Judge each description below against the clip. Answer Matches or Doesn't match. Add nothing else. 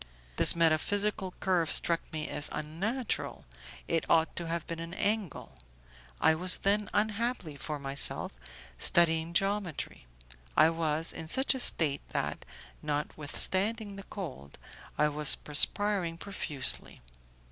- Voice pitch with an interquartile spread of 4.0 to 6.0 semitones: Matches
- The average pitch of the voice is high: Doesn't match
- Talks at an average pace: Doesn't match